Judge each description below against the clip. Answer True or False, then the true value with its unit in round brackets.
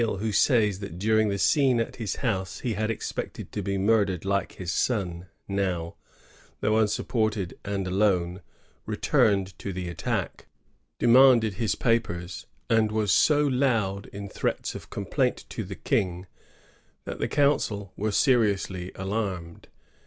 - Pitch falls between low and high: False (100 Hz)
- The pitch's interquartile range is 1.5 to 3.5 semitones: True (3.1 semitones)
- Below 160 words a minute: True (145 wpm)